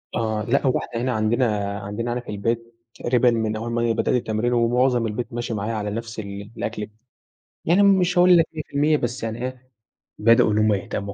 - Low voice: Yes, low, 115 Hz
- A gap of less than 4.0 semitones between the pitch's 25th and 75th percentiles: Yes, narrow, 2.6 semitones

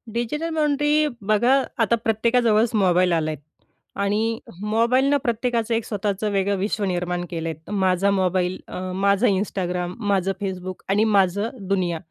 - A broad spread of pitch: No, average, 3.7 semitones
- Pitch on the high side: Yes, high, 200 Hz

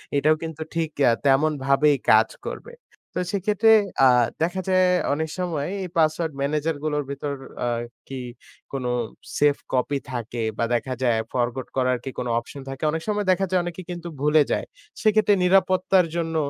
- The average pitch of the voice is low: No, medium, 155 Hz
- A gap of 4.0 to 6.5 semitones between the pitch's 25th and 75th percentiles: Yes, average, 4.6 semitones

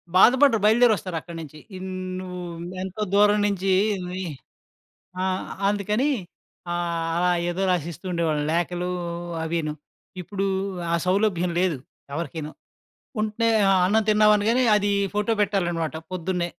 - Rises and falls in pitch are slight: No, average, 3.4 semitones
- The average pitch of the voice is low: No, medium, 185 Hz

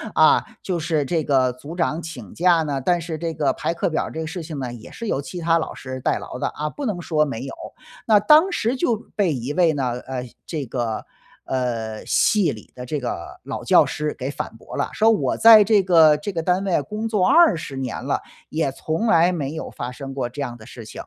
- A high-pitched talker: No, medium, 155 Hz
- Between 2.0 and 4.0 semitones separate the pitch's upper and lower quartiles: No, average, 5.2 semitones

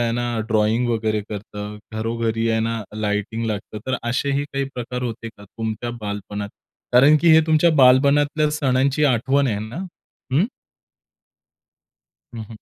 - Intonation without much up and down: No, average, 4.0 semitones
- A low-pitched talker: Yes, low, 115 Hz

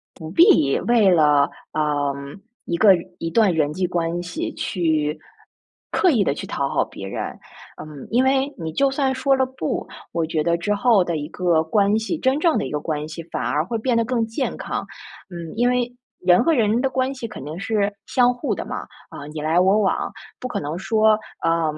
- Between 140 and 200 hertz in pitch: Yes, high, 195 Hz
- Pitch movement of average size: No, wide, 7.4 semitones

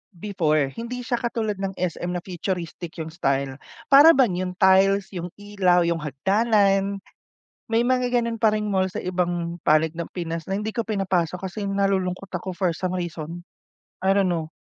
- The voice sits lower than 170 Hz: No, medium, 185 Hz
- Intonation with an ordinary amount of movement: Yes, average, 3.0 semitones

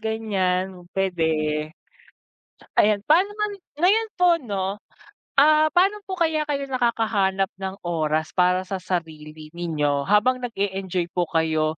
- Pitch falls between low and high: No, high, 195 Hz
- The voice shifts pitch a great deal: Yes, wide, 7.2 semitones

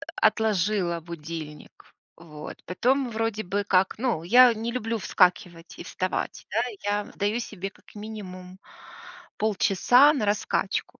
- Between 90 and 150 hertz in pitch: No, high, 205 Hz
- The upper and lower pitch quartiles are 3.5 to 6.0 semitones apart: Yes, average, 3.8 semitones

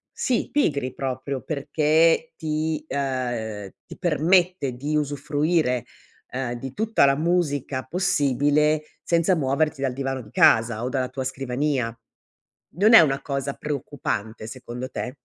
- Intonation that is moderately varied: Yes, average, 3.3 semitones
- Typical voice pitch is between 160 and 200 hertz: No, medium, 140 Hz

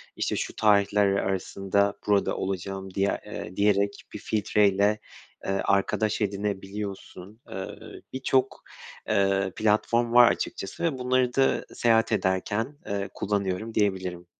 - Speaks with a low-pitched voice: Yes, low, 100 Hz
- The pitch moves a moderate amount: No, narrow, 2.0 semitones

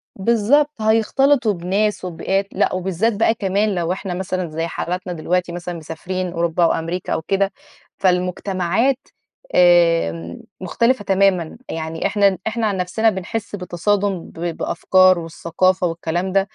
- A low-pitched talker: No, medium, 185 Hz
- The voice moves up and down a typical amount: Yes, average, 3.0 semitones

